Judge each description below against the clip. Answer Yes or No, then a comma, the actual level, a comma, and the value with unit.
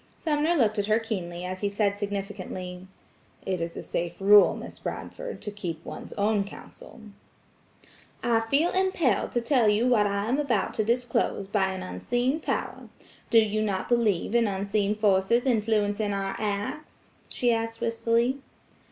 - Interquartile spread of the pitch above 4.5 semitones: No, average, 3.0 semitones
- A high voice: Yes, high, 215 Hz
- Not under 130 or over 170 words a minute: Yes, average, 160 wpm